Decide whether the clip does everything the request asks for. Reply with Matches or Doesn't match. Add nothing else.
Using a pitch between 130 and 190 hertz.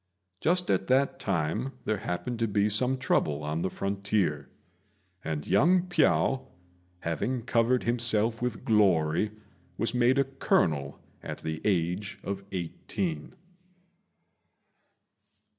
Doesn't match